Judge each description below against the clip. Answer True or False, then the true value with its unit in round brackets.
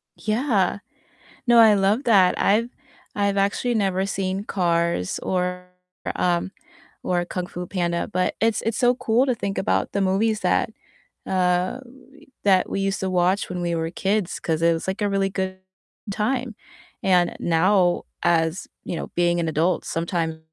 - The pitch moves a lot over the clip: False (2.8 semitones)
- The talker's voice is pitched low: False (190 Hz)